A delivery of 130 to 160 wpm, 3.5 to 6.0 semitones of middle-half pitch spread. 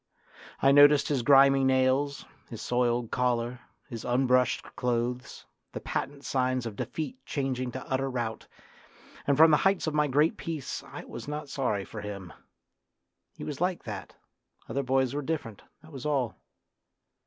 No: average, 155 wpm; average, 2.9 semitones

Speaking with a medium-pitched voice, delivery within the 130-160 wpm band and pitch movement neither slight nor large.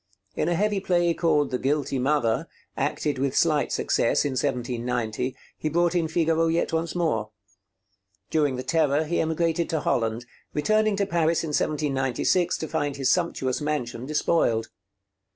Yes: medium, 150 Hz; average, 150 wpm; average, 4.2 semitones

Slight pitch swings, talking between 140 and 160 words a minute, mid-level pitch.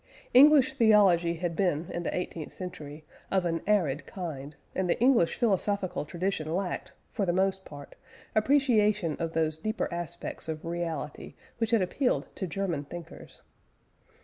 No: average, 4.2 semitones; average, 145 wpm; medium, 180 Hz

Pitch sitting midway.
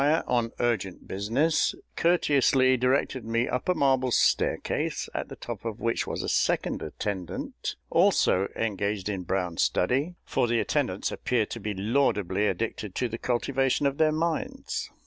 No: low, 120 Hz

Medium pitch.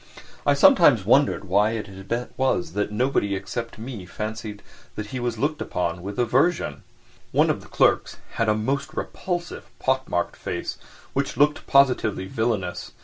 No: low, 115 Hz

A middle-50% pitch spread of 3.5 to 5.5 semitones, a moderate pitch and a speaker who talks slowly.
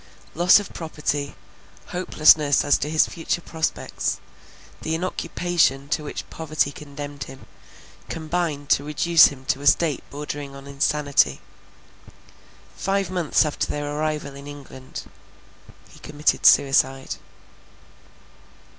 No: narrow, 2.4 semitones; medium, 150 Hz; slow, 115 wpm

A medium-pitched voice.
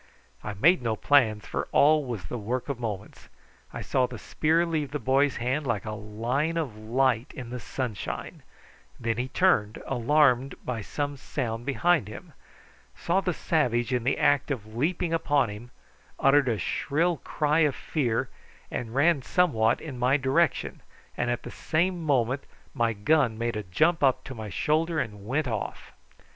No: low, 130 Hz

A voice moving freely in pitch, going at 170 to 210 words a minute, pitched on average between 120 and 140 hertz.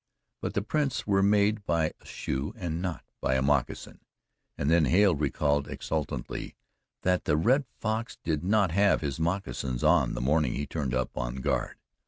No: wide, 5.9 semitones; average, 175 wpm; very low, 80 Hz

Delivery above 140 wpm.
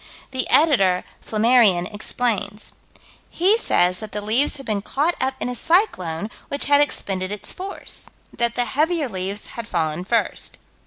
Yes: average, 155 wpm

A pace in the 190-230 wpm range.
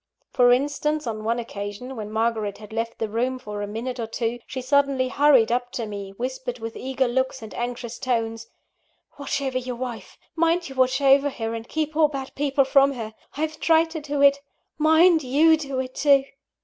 Yes: average, 200 wpm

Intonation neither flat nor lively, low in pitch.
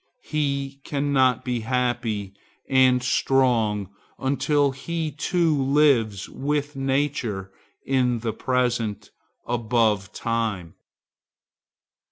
Yes: average, 3.6 semitones; low, 125 Hz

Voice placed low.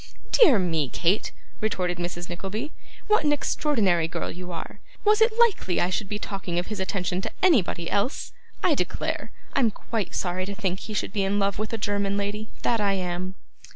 No: high, 200 Hz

